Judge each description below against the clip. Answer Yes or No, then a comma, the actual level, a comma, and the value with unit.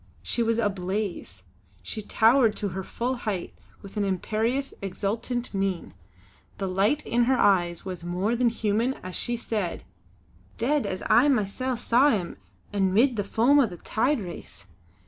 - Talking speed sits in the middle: Yes, average, 160 wpm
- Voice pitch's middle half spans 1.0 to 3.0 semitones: No, average, 4.0 semitones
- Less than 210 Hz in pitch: No, high, 215 Hz